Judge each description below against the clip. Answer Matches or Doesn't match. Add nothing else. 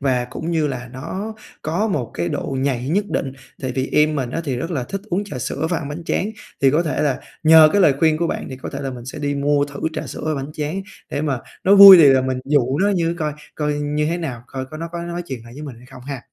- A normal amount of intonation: Matches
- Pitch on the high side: Doesn't match